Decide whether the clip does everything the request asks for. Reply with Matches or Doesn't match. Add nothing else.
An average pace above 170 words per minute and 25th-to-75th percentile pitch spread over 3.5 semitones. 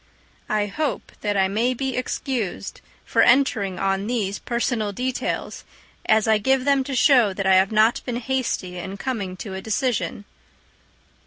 Doesn't match